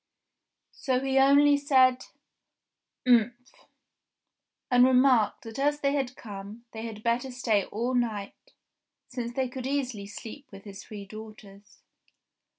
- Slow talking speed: Yes, slow, 130 wpm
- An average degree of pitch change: Yes, average, 3.6 semitones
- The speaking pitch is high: Yes, high, 245 Hz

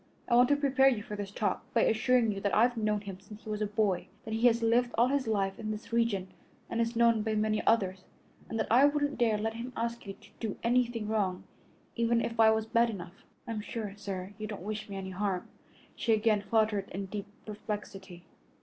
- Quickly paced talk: Yes, fast, 225 wpm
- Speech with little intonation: Yes, narrow, 2.3 semitones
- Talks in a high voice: Yes, high, 215 Hz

